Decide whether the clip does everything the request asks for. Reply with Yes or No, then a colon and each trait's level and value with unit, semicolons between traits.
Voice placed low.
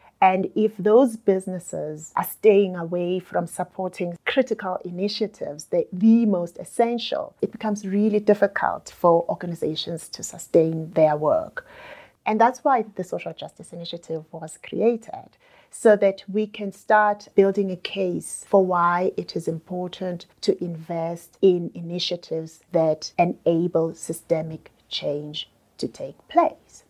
No: medium, 185 Hz